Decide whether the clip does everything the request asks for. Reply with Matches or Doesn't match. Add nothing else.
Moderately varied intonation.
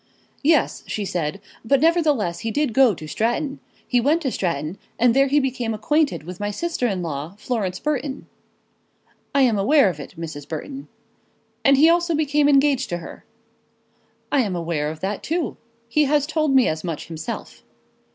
Doesn't match